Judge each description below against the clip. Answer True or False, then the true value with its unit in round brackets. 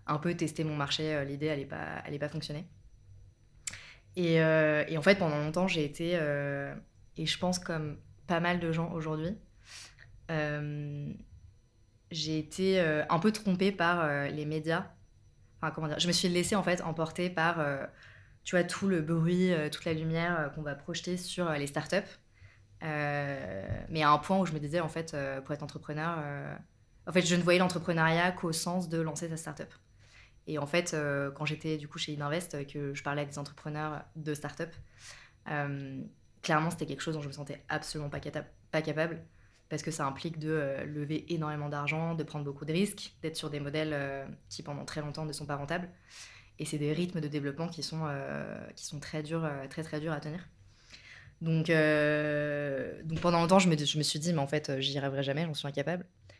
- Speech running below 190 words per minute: False (210 wpm)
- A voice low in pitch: False (150 Hz)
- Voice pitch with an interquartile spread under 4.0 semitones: True (2.7 semitones)